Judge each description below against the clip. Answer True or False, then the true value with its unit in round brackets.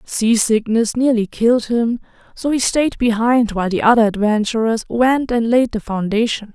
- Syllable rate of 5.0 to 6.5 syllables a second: False (4.8 syllables/s)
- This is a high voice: True (230 Hz)